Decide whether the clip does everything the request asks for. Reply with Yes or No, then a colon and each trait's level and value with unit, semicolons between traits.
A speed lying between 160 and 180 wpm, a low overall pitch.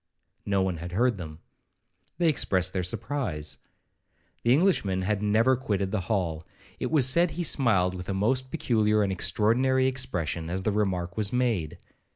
Yes: average, 165 wpm; low, 105 Hz